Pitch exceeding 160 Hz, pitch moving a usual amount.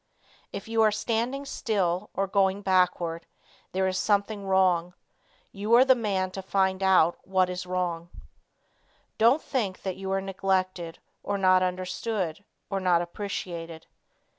No: high, 190 Hz; narrow, 1.9 semitones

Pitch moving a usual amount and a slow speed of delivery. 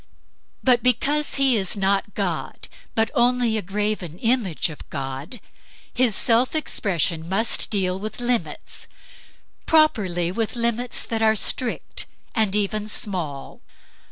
Yes: average, 4.4 semitones; slow, 125 wpm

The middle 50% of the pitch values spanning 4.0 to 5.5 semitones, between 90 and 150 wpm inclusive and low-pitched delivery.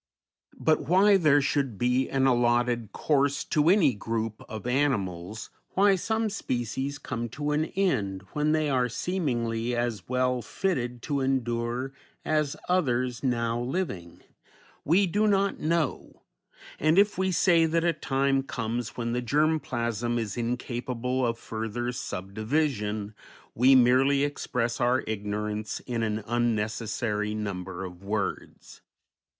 Yes: average, 4.6 semitones; slow, 135 wpm; low, 125 Hz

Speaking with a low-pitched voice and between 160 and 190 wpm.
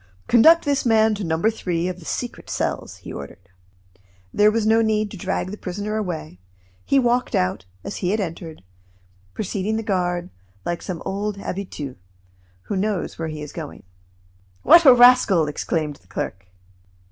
No: high, 195 Hz; average, 165 wpm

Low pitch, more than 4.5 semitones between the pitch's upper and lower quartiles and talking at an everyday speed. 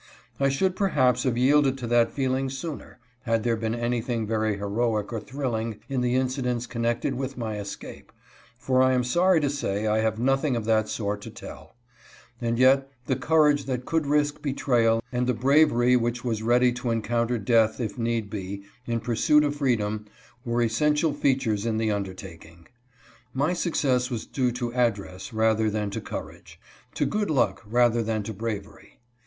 No: low, 120 Hz; average, 3.2 semitones; average, 175 wpm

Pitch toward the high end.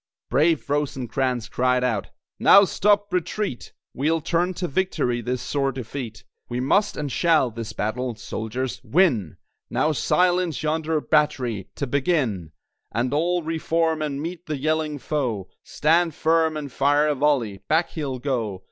No: medium, 145 Hz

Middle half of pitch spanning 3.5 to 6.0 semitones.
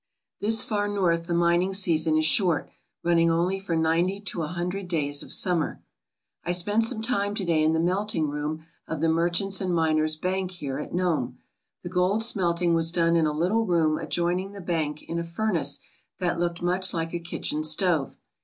No: average, 2.7 semitones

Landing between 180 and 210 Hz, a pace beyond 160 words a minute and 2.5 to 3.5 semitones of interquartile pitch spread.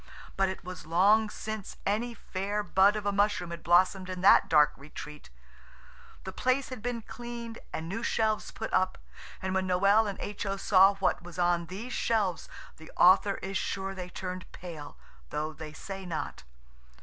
Yes: high, 190 Hz; average, 175 wpm; average, 2.9 semitones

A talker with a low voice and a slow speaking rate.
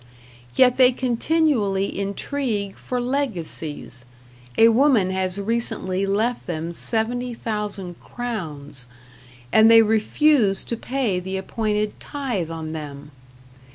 No: high, 210 Hz; slow, 105 wpm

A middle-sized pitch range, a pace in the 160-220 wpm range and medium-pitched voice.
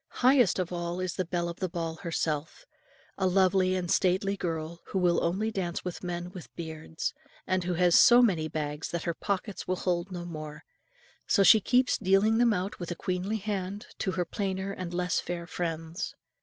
No: narrow, 2.2 semitones; average, 195 wpm; medium, 180 Hz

